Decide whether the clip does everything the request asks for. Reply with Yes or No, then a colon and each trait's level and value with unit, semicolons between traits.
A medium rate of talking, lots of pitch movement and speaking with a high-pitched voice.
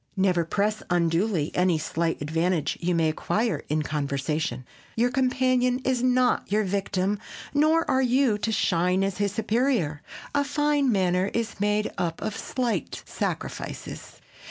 Yes: average, 145 wpm; wide, 6.7 semitones; high, 200 Hz